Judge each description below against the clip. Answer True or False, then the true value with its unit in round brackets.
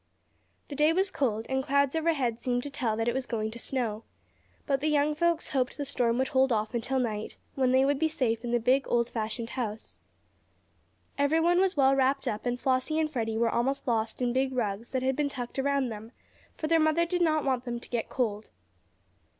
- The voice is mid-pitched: False (260 Hz)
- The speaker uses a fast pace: True (215 wpm)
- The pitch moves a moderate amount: True (3.4 semitones)